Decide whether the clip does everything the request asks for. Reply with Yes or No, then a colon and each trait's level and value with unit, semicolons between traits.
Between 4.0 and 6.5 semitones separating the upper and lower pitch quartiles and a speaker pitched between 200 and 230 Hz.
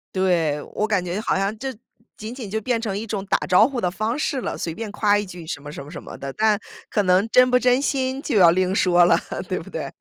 Yes: average, 4.3 semitones; high, 205 Hz